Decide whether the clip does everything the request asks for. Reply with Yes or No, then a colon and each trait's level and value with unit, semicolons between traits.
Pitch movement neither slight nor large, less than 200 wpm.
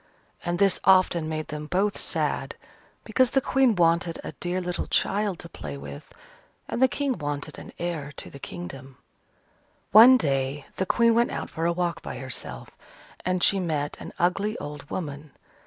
Yes: average, 5.0 semitones; average, 170 wpm